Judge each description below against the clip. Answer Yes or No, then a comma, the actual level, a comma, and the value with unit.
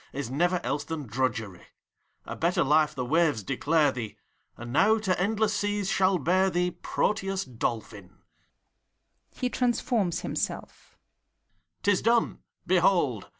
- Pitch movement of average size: No, wide, 6.7 semitones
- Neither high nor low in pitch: Yes, medium, 170 Hz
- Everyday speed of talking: No, slow, 130 wpm